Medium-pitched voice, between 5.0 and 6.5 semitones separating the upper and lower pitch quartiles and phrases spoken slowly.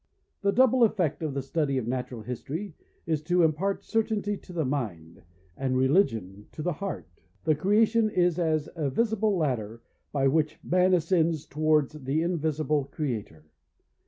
No: medium, 155 Hz; average, 5.3 semitones; average, 155 wpm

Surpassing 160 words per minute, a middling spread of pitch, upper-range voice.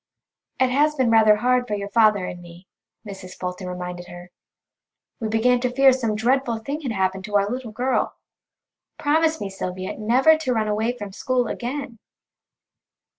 Yes: average, 170 wpm; average, 4.5 semitones; high, 225 Hz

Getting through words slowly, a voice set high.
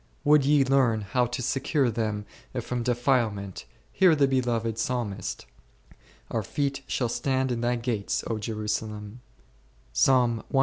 No: slow, 130 wpm; low, 120 Hz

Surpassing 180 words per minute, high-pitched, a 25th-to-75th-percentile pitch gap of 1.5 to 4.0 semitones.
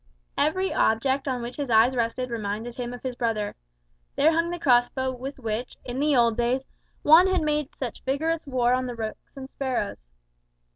Yes: average, 190 wpm; very high, 255 Hz; average, 3.0 semitones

